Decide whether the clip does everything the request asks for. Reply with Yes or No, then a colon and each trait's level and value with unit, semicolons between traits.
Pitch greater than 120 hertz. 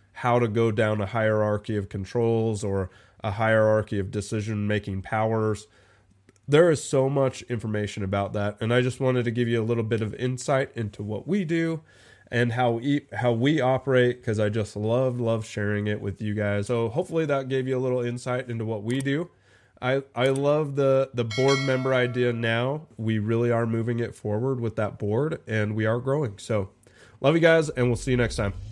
No: low, 115 Hz